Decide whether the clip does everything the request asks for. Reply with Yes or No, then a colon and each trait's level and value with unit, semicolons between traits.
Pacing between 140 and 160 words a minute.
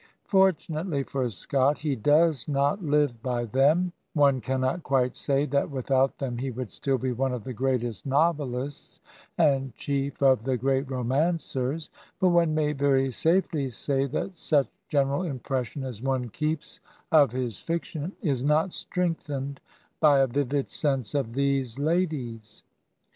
Yes: average, 150 wpm